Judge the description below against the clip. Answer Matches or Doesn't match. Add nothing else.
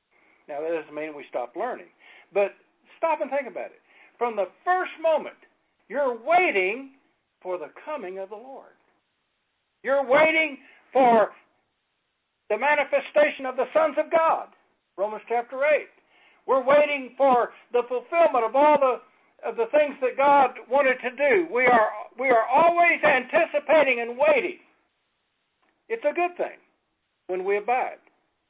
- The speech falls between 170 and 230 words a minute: Doesn't match